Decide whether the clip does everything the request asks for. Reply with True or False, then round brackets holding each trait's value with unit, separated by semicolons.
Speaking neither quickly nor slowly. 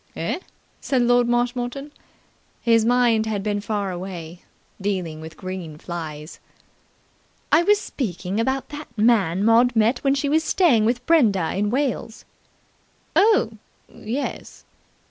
False (125 wpm)